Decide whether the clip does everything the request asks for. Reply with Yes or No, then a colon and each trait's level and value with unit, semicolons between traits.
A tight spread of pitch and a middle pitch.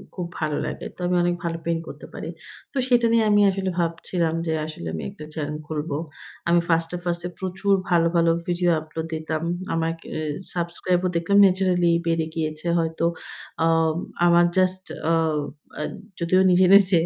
Yes: narrow, 2.0 semitones; medium, 170 Hz